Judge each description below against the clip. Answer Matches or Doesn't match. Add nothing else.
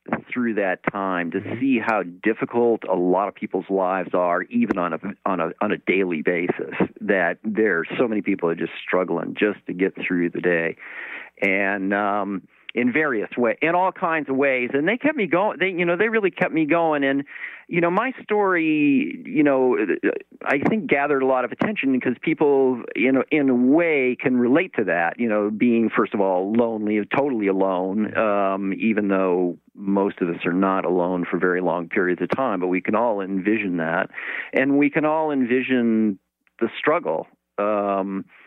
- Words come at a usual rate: Matches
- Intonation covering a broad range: Matches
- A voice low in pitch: Matches